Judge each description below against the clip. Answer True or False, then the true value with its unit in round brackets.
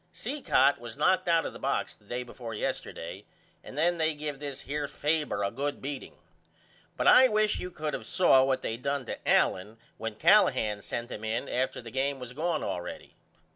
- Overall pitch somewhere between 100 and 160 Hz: True (140 Hz)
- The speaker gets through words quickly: False (195 wpm)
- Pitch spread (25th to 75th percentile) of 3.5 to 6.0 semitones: True (5.0 semitones)